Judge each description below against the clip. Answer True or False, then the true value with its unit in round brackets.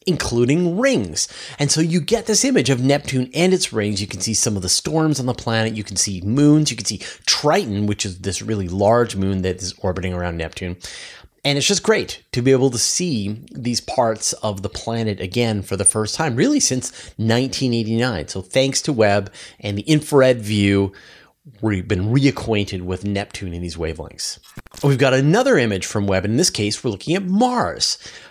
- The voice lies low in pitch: True (110 Hz)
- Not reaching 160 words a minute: False (200 wpm)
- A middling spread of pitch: False (5.7 semitones)